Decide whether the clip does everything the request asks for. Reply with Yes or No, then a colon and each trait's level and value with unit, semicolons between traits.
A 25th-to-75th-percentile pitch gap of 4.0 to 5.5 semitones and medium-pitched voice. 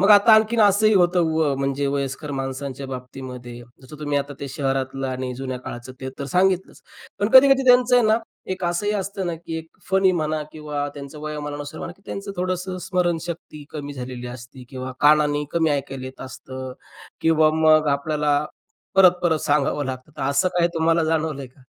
Yes: average, 4.7 semitones; medium, 150 Hz